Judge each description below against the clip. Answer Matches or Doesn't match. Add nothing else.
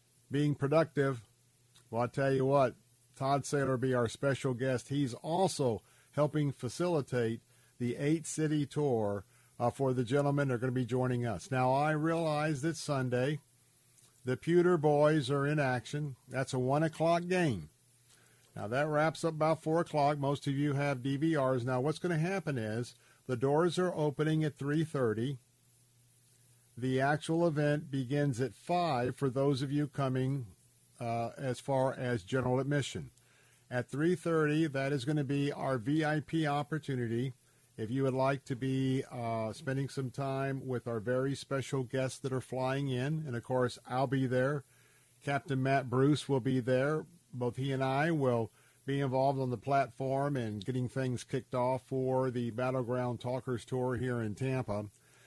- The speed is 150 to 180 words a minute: Matches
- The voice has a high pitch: Doesn't match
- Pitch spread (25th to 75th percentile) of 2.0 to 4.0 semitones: Matches